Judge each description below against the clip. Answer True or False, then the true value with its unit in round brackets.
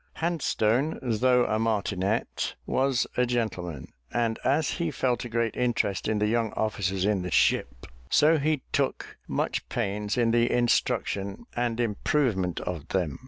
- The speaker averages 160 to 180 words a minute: False (150 wpm)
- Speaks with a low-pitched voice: True (115 Hz)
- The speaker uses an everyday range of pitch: True (3.9 semitones)